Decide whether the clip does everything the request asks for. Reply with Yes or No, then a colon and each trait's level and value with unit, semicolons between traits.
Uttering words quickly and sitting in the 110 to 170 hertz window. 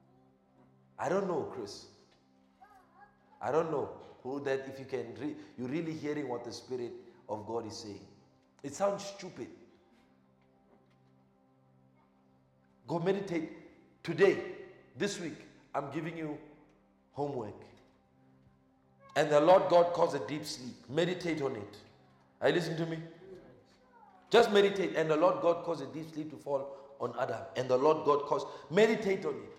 No: average, 150 wpm; medium, 140 Hz